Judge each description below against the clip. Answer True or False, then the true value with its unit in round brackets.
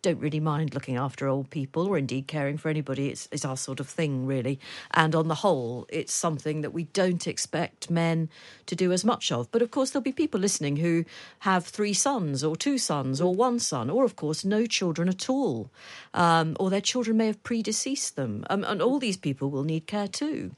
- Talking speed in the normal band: False (220 wpm)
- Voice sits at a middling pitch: True (170 Hz)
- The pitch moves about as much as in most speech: False (6.1 semitones)